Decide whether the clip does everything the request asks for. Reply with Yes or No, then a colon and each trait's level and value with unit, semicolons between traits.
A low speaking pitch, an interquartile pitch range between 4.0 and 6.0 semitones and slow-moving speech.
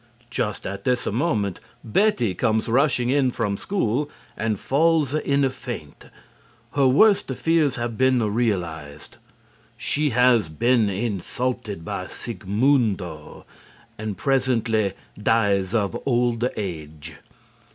Yes: low, 115 Hz; average, 4.7 semitones; slow, 110 wpm